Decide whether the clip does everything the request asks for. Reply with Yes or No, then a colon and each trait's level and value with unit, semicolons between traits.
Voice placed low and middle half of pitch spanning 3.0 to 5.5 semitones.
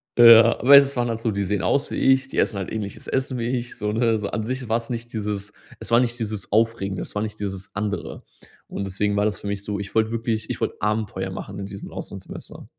No: low, 110 Hz; narrow, 2.5 semitones